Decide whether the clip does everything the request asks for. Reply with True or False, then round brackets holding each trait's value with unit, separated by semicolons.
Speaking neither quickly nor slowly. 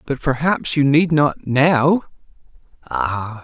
False (105 wpm)